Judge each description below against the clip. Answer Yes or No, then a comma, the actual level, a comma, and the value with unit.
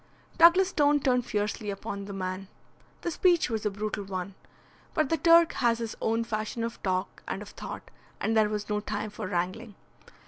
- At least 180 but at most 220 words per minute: Yes, average, 185 wpm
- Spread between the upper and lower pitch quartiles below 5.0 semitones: Yes, average, 3.9 semitones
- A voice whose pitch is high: Yes, high, 215 Hz